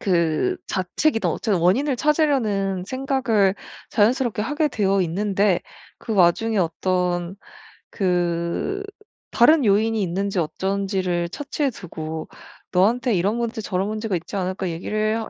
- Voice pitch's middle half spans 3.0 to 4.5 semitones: Yes, average, 4.2 semitones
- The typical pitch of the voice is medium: No, high, 200 Hz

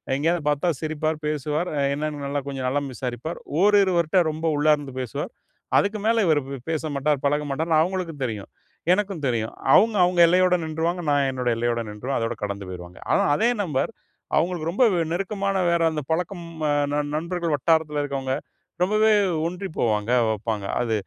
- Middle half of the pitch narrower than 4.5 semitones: No, average, 4.8 semitones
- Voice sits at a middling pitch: Yes, medium, 155 Hz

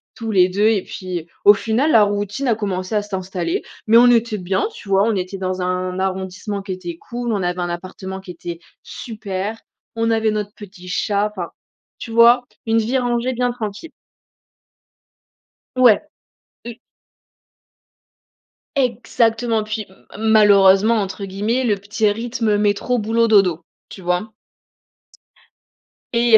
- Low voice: No, high, 210 Hz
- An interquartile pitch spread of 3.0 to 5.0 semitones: Yes, average, 3.3 semitones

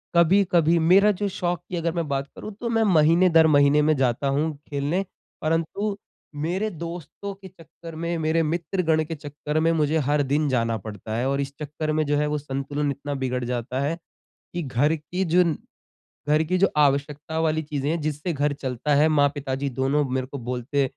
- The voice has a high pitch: No, medium, 150 Hz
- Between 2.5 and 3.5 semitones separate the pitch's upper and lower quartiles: Yes, average, 3.0 semitones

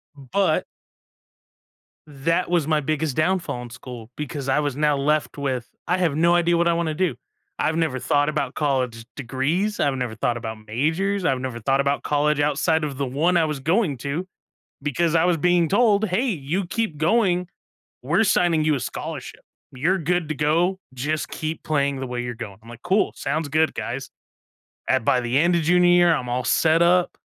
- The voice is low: No, medium, 150 Hz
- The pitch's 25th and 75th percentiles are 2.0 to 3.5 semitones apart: No, average, 4.3 semitones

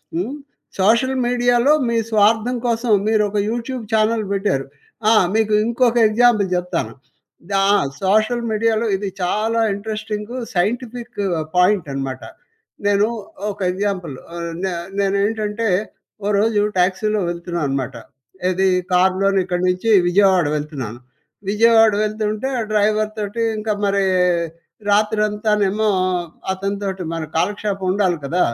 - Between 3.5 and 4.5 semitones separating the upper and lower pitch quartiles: No, average, 2.9 semitones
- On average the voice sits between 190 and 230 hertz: Yes, high, 210 Hz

